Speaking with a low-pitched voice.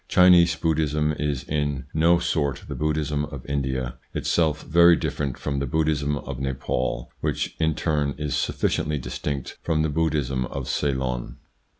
Yes: very low, 75 Hz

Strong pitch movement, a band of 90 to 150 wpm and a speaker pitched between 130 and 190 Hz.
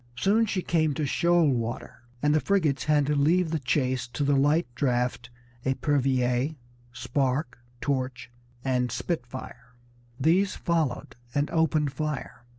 No: average, 3.8 semitones; slow, 135 wpm; medium, 140 Hz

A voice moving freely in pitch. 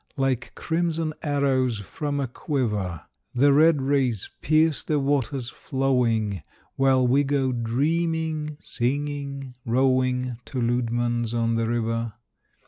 No: average, 3.3 semitones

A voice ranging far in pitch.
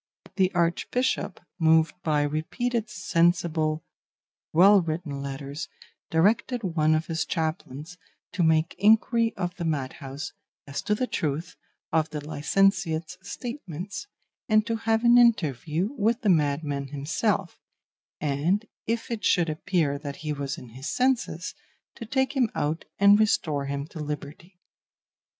Yes: wide, 5.8 semitones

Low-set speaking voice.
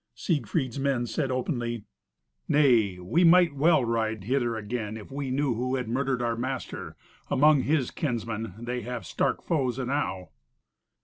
Yes: low, 125 Hz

